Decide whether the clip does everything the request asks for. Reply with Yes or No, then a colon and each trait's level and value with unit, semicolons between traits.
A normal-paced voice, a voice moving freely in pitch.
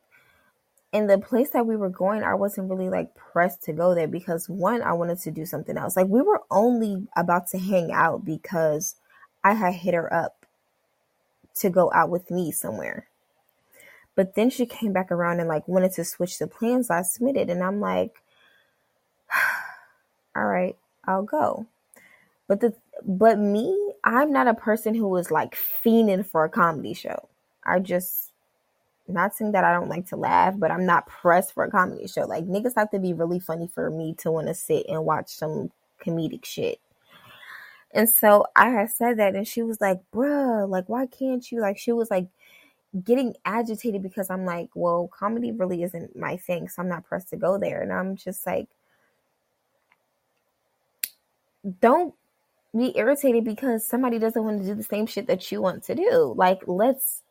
No: average, 185 wpm; average, 4.7 semitones